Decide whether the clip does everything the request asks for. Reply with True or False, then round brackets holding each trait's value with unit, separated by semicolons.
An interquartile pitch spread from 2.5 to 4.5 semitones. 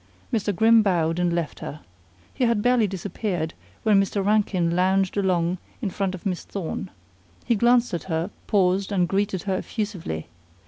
True (3.0 semitones)